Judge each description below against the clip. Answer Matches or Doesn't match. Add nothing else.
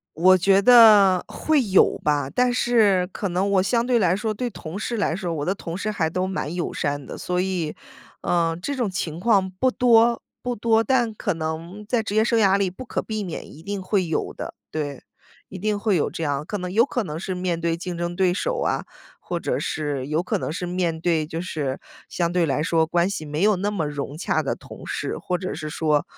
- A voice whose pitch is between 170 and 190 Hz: Matches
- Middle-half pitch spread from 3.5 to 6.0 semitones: Matches